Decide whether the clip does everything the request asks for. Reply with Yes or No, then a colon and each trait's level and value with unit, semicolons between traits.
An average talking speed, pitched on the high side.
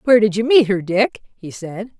No: fast, 240 wpm; high, 210 Hz